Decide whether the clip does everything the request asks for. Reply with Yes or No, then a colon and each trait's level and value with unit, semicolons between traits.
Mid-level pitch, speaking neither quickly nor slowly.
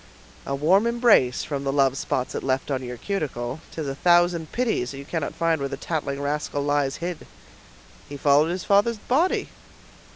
Yes: medium, 145 Hz; average, 185 wpm